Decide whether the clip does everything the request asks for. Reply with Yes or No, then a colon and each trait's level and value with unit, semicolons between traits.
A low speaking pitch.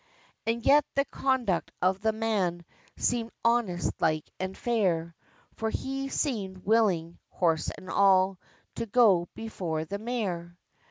No: high, 200 Hz